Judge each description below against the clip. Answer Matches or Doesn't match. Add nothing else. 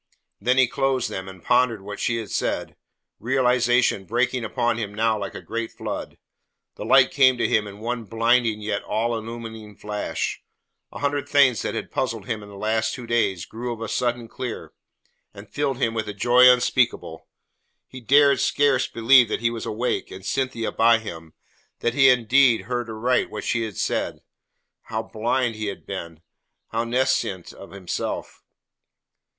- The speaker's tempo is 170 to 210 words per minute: Matches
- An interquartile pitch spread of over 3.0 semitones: Doesn't match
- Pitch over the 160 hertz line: Doesn't match